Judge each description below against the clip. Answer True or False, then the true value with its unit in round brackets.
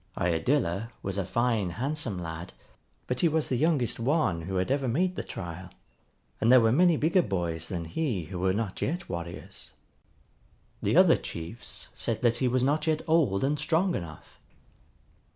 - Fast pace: False (170 wpm)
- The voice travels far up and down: True (8.8 semitones)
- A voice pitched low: True (115 Hz)